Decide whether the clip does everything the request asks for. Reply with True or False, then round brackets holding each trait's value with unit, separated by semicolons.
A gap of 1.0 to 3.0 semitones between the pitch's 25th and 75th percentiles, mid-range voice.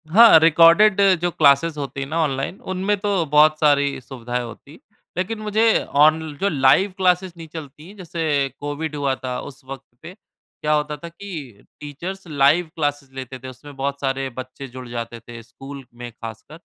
False (4.0 semitones; 145 Hz)